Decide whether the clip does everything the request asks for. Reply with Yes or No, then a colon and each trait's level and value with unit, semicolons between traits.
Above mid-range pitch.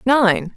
Yes: high, 205 Hz